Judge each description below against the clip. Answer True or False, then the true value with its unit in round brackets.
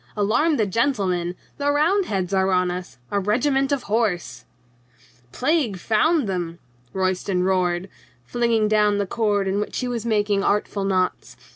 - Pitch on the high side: True (205 Hz)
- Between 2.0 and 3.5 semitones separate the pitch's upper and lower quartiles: False (4.3 semitones)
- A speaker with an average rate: True (155 wpm)